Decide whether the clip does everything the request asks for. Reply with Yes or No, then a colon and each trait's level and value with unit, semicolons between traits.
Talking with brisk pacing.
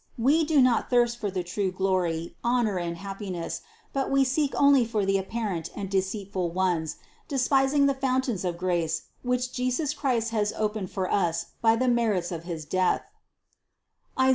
No: average, 165 wpm